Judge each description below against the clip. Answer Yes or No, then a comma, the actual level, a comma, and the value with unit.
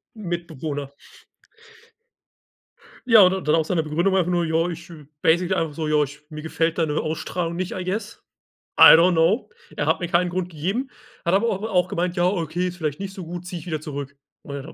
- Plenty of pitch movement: No, narrow, 2.5 semitones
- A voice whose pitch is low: No, medium, 170 Hz